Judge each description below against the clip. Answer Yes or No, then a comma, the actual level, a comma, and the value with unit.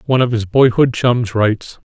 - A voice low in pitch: Yes, low, 120 Hz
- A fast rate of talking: No, average, 190 wpm